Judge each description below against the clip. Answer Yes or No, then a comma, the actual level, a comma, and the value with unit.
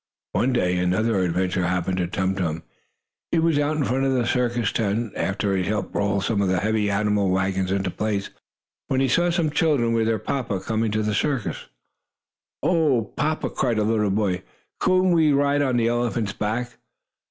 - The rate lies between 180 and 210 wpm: Yes, average, 190 wpm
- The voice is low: Yes, low, 110 Hz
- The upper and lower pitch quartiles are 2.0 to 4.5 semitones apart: No, average, 5.2 semitones